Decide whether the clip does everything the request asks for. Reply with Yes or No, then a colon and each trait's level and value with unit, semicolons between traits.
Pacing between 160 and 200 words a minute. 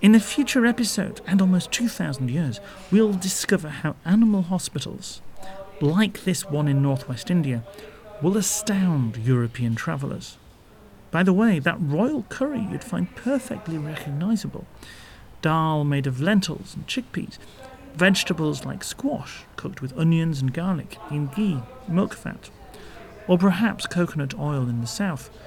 No: slow, 135 wpm